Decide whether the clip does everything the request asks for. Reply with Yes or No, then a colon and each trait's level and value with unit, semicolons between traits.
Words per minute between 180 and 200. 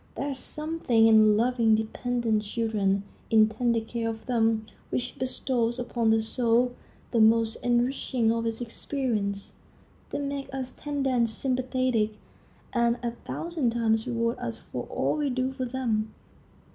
No: average, 145 wpm